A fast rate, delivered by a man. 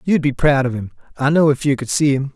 Yes: fast, 305 wpm; male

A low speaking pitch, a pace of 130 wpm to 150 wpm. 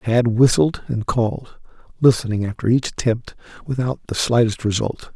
Yes: low, 120 Hz; average, 140 wpm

